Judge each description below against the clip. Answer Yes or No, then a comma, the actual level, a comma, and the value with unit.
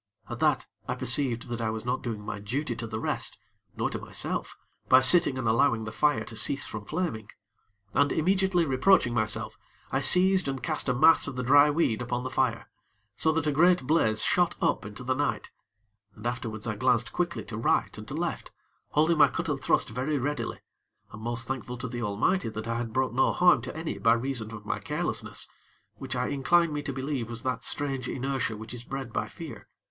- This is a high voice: No, low, 130 Hz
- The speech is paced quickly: Yes, fast, 210 wpm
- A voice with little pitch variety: No, average, 4.2 semitones